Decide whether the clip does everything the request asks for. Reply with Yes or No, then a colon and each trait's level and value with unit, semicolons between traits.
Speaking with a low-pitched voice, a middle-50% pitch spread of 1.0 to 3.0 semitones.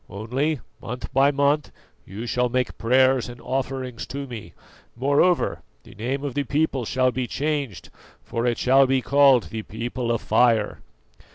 Yes: low, 130 Hz; narrow, 2.6 semitones